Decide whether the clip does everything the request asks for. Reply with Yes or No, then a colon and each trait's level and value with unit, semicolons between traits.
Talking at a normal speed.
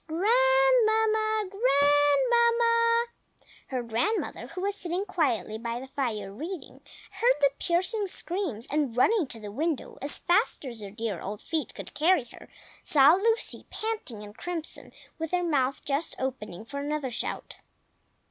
Yes: average, 145 wpm